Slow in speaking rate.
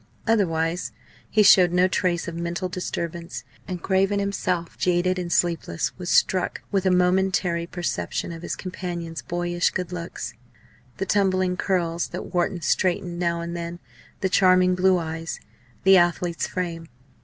No: average, 145 wpm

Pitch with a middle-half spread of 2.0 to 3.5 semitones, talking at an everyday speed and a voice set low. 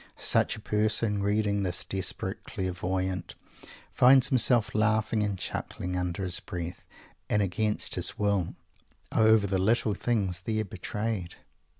No: average, 2.8 semitones; slow, 125 wpm; low, 100 Hz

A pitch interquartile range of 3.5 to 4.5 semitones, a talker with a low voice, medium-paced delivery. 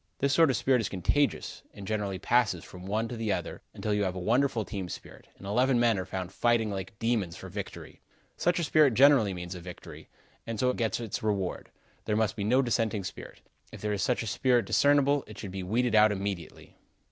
No: average, 4.1 semitones; low, 110 Hz; fast, 215 wpm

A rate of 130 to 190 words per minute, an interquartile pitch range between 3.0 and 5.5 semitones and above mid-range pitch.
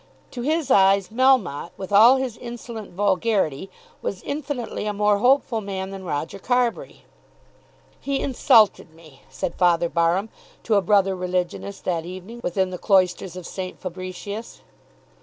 Yes: average, 140 wpm; average, 4.1 semitones; high, 195 Hz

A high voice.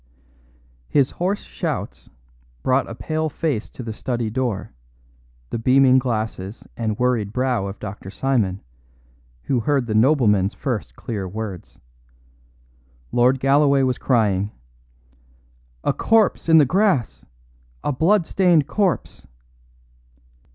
No: low, 125 Hz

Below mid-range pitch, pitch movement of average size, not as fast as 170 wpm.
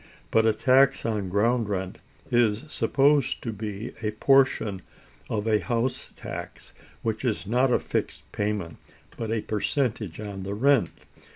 Yes: low, 110 Hz; average, 3.3 semitones; average, 150 wpm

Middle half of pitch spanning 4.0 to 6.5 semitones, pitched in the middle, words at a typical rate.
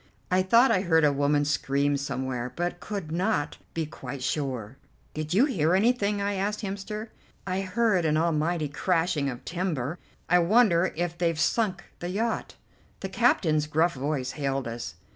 Yes: average, 5.0 semitones; medium, 170 Hz; average, 160 wpm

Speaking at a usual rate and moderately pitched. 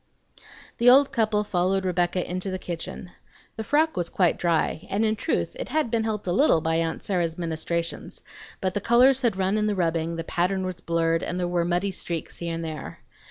No: fast, 210 wpm; medium, 180 Hz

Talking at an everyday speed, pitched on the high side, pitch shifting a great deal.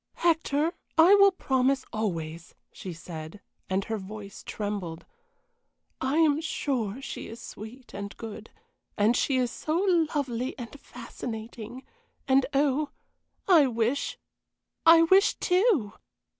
No: slow, 120 wpm; very high, 255 Hz; wide, 6.5 semitones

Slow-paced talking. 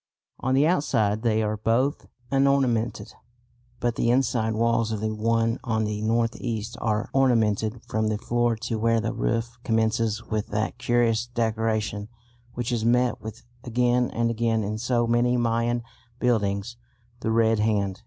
No: average, 155 wpm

